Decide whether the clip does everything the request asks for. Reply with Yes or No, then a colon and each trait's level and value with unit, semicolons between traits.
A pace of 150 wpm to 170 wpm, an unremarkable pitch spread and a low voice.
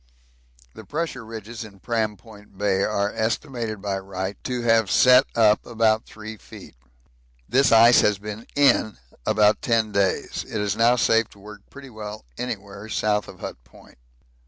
No: average, 160 wpm; narrow, 2.1 semitones; low, 110 Hz